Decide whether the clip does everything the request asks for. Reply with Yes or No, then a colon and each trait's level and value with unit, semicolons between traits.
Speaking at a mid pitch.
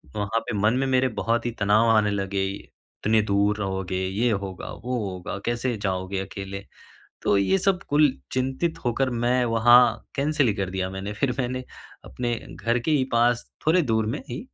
No: low, 115 Hz